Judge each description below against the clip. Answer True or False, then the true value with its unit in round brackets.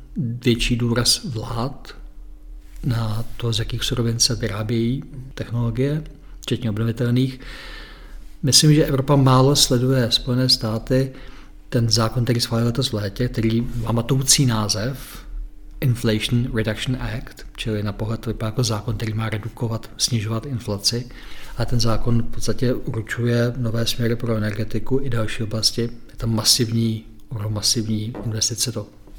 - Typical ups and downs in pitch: False (2.3 semitones)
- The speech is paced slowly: False (135 wpm)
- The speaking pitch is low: True (115 Hz)